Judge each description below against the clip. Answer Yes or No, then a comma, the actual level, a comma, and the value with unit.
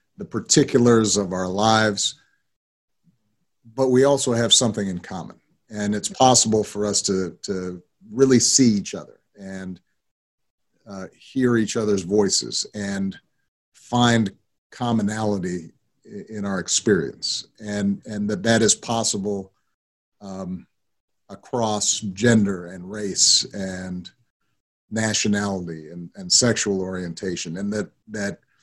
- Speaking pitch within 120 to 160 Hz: No, low, 105 Hz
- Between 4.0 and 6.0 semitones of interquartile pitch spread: No, average, 3.5 semitones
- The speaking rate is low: Yes, slow, 115 wpm